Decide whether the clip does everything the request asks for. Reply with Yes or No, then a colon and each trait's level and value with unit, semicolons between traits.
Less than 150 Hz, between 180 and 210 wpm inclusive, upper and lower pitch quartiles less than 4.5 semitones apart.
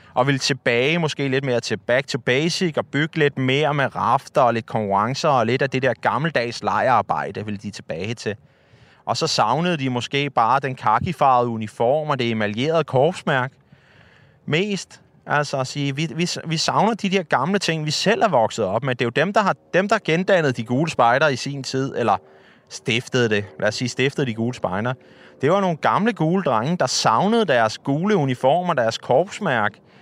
No: low, 135 Hz; average, 195 wpm; average, 5.2 semitones